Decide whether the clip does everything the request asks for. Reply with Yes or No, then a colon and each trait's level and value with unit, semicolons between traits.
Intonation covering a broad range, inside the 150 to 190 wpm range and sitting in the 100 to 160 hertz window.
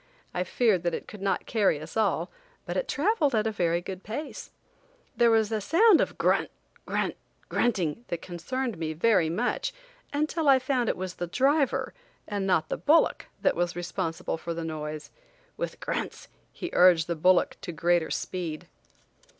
No: wide, 6.4 semitones; average, 175 wpm; high, 190 Hz